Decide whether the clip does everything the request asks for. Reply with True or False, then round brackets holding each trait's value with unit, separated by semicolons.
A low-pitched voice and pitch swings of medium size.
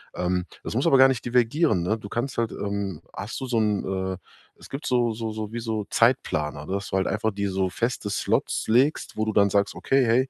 True (110 Hz; 3.6 semitones)